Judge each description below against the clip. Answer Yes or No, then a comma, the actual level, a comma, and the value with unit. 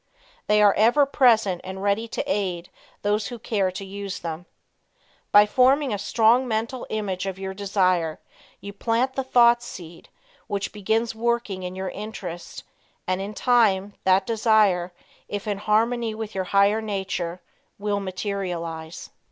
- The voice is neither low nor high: No, high, 205 Hz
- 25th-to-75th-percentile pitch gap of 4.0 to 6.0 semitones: No, average, 3.0 semitones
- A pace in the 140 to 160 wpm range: Yes, average, 150 wpm